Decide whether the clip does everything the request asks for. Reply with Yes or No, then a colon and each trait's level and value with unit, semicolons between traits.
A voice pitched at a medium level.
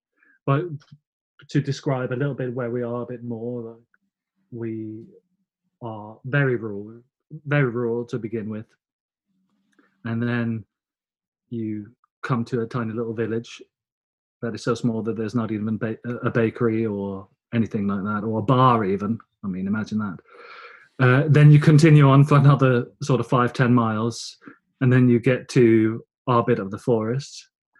No: low, 120 Hz